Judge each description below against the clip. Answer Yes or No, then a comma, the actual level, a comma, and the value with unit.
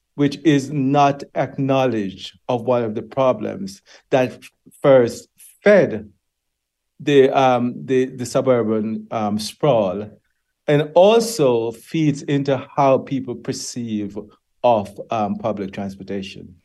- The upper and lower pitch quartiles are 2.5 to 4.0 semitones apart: No, average, 4.5 semitones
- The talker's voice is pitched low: Yes, low, 125 Hz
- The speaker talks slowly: Yes, slow, 110 wpm